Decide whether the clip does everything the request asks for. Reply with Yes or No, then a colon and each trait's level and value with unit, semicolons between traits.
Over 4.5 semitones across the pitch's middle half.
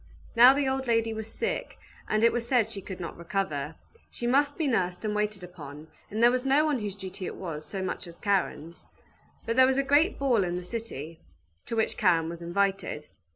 Yes: wide, 5.5 semitones